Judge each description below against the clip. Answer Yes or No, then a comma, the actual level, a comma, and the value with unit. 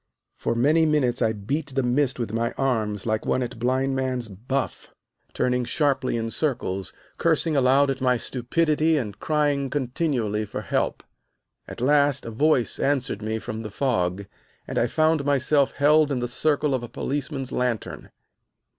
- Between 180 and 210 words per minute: No, average, 165 wpm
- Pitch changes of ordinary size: Yes, average, 3.7 semitones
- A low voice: Yes, low, 130 Hz